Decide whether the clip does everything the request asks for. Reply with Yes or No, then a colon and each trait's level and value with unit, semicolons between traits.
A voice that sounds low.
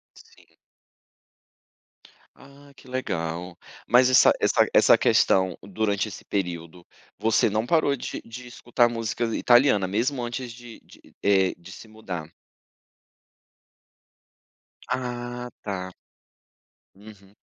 Yes: low, 110 Hz